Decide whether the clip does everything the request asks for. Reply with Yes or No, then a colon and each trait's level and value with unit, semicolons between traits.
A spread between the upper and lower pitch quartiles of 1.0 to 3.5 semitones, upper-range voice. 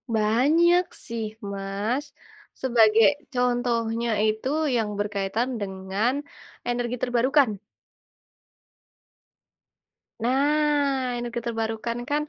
Yes: average, 3.0 semitones; high, 235 Hz